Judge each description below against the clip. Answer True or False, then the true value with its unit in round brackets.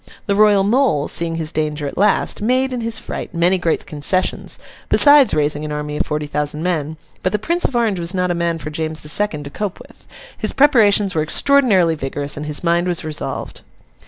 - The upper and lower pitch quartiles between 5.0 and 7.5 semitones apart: True (5.6 semitones)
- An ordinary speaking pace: False (210 wpm)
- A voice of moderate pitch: True (170 Hz)